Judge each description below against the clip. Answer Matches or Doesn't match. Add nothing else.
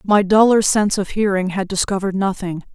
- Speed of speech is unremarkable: Matches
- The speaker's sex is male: Doesn't match